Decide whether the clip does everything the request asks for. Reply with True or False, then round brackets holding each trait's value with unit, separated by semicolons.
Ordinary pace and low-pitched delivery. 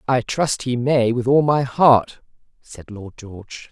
True (180 wpm; 125 Hz)